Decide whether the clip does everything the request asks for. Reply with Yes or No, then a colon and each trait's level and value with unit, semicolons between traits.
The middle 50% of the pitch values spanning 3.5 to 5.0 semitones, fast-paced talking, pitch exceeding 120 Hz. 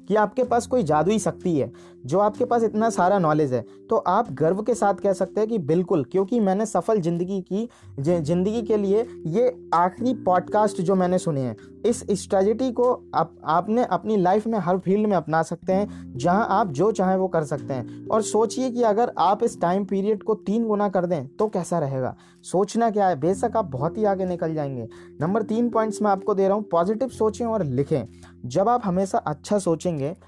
Yes: average, 4.6 semitones; fast, 205 wpm; high, 190 Hz